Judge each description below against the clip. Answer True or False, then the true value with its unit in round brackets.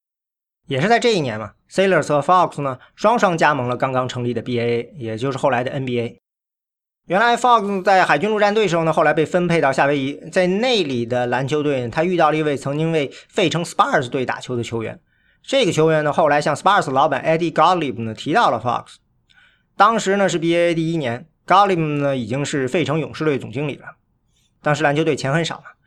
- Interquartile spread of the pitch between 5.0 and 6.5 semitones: True (5.4 semitones)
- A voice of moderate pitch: True (150 Hz)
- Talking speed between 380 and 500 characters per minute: True (385 characters per minute)